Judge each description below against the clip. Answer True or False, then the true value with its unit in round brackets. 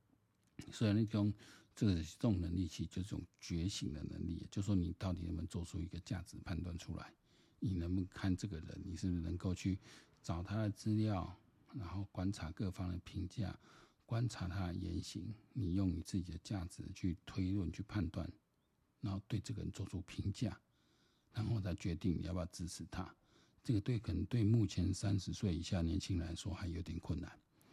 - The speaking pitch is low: True (95 Hz)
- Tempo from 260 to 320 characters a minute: True (290 characters per minute)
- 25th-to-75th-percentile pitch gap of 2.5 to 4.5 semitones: True (3.0 semitones)